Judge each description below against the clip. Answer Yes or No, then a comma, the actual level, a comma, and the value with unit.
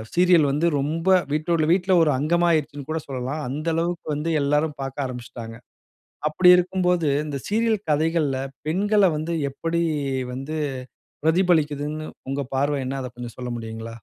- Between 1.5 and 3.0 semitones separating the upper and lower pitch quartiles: No, average, 3.7 semitones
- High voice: No, medium, 155 Hz